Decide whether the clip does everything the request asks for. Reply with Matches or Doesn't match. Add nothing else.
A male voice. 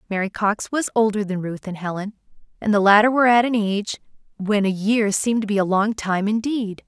Doesn't match